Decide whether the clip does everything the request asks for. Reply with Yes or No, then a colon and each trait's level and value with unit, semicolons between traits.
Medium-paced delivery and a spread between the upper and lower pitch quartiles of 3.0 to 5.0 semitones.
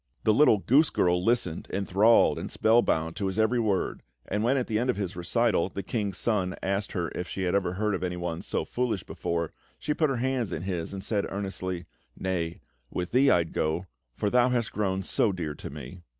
No: fast, 210 wpm; average, 4.2 semitones